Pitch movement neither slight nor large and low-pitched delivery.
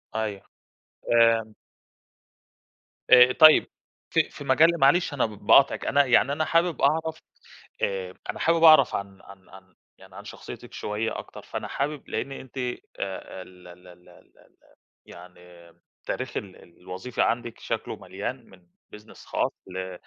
No: wide, 6.8 semitones; low, 110 Hz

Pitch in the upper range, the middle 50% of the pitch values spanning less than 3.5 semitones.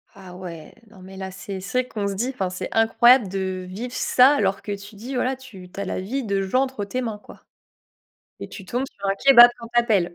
No: high, 205 Hz; average, 4.5 semitones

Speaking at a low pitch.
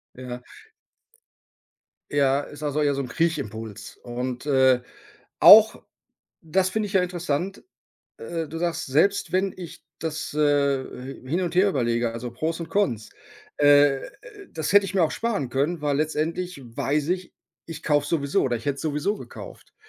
No: medium, 150 Hz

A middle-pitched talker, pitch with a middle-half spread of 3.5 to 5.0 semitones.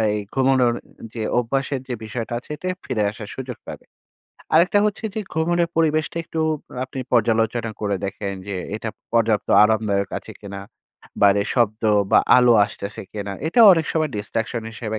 No: low, 115 Hz; average, 4.5 semitones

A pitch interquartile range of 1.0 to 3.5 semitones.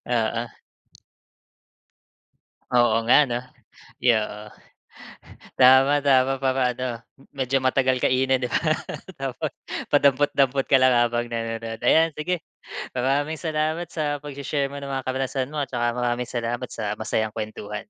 Yes: average, 2.8 semitones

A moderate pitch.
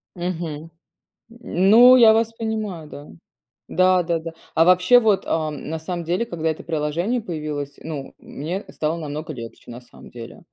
Yes: medium, 165 Hz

